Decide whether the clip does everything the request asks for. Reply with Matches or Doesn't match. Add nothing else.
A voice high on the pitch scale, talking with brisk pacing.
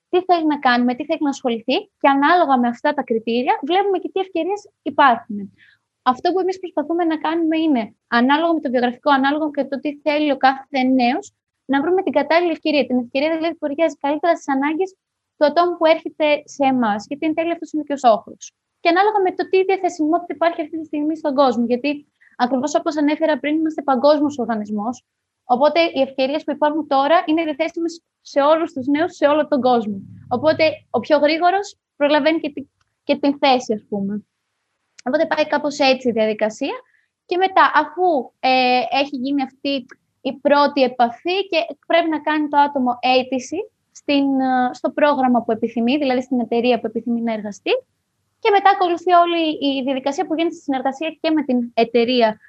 Matches